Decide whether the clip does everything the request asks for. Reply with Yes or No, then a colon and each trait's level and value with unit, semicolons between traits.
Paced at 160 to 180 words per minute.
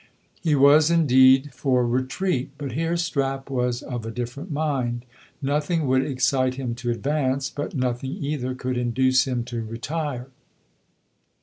No: average, 140 wpm